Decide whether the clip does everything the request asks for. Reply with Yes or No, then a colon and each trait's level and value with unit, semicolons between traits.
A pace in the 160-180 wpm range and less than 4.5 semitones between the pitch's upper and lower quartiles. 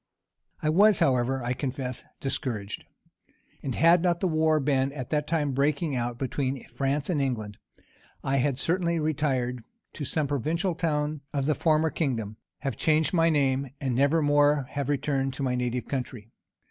Yes: average, 165 wpm; average, 3.2 semitones